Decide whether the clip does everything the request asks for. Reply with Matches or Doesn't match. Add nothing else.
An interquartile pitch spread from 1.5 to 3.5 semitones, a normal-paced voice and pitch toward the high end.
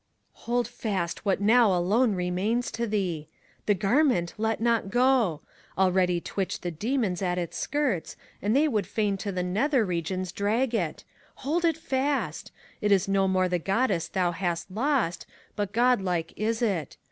Doesn't match